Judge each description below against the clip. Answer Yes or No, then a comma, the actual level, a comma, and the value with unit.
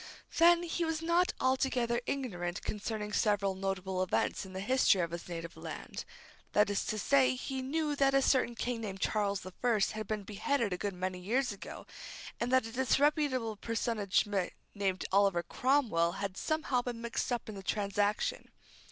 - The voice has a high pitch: Yes, high, 215 Hz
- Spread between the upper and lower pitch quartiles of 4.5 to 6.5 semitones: Yes, average, 5.1 semitones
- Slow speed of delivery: No, average, 175 wpm